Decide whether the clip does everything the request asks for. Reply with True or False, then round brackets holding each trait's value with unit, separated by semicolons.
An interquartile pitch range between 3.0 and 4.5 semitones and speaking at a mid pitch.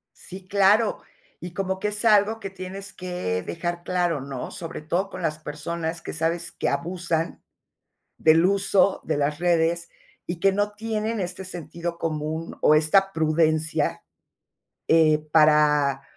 True (3.5 semitones; 170 Hz)